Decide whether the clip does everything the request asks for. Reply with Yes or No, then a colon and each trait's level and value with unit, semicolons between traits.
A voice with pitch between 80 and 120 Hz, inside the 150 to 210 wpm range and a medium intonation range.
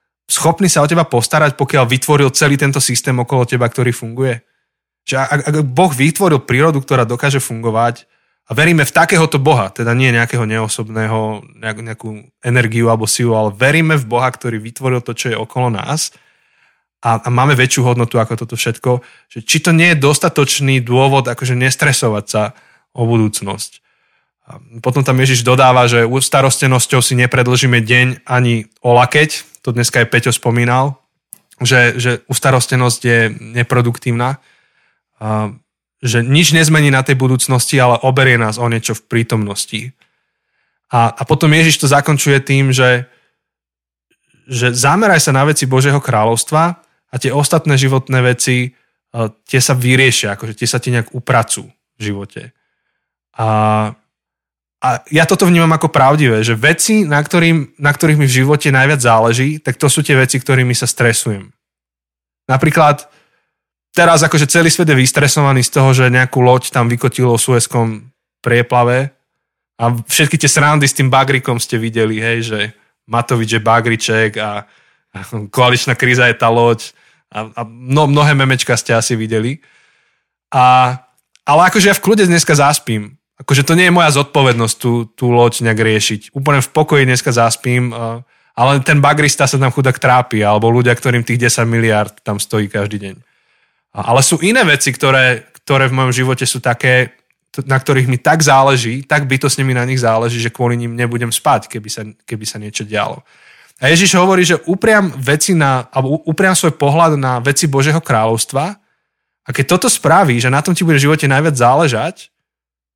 No: low, 130 Hz; fast, 165 wpm; average, 3.6 semitones